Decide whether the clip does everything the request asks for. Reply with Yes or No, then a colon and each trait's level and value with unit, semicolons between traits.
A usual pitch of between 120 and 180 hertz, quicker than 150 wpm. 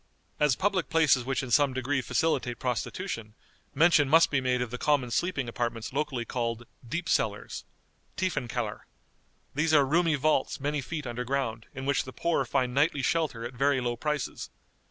Yes: low, 135 Hz; average, 175 wpm